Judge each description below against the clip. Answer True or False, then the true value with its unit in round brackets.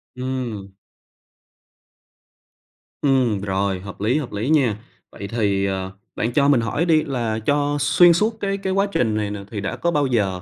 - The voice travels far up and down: True (6.2 semitones)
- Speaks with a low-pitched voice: True (120 Hz)